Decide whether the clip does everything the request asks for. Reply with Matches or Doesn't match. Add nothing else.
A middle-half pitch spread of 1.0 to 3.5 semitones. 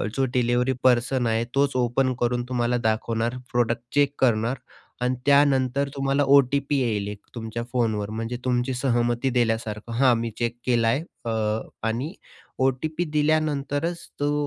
Matches